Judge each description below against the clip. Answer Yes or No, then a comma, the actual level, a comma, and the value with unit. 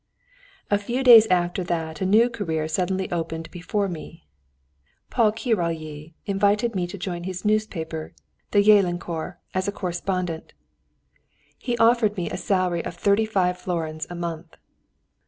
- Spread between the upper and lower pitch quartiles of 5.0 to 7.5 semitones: No, average, 3.5 semitones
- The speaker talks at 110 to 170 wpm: Yes, average, 140 wpm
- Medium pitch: Yes, medium, 180 Hz